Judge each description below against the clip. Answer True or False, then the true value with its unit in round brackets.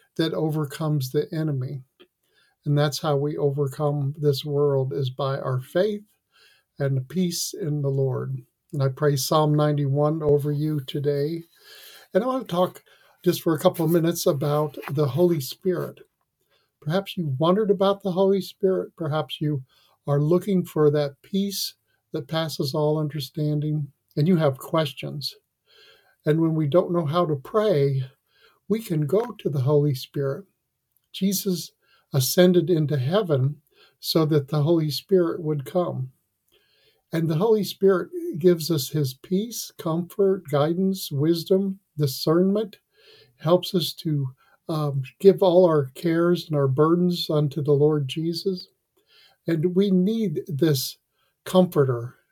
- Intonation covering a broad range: False (4.0 semitones)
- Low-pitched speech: False (155 Hz)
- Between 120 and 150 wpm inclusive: True (140 wpm)